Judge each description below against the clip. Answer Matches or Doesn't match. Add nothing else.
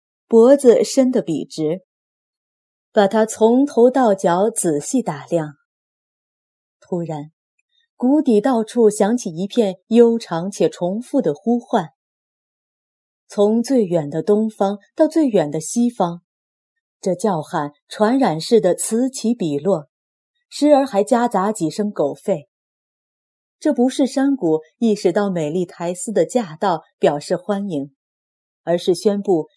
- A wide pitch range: Matches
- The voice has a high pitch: Matches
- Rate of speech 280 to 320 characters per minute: Doesn't match